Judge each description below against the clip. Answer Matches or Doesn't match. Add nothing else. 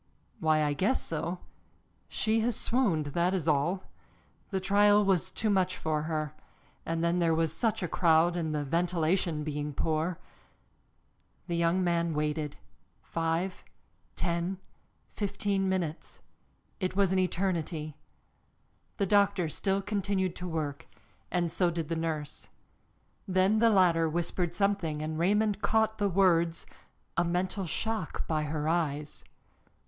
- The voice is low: Doesn't match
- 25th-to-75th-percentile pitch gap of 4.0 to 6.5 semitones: Doesn't match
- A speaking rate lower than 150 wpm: Matches